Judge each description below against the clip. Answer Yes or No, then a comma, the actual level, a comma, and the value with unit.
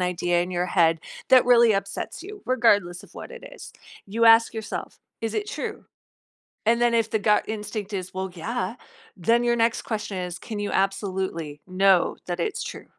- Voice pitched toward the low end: No, high, 205 Hz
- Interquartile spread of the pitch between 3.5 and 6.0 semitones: Yes, average, 4.2 semitones